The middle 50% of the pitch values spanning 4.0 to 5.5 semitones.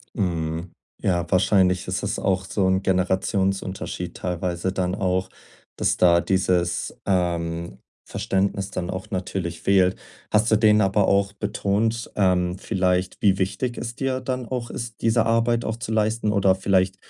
No: average, 2.7 semitones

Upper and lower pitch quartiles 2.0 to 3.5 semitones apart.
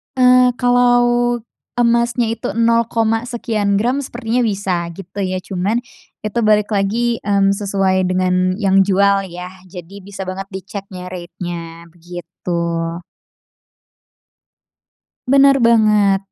No: average, 3.9 semitones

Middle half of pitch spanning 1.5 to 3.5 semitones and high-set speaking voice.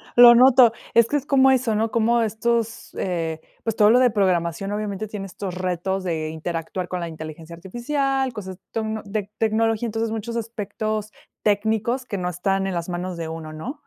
No: average, 4.3 semitones; high, 210 Hz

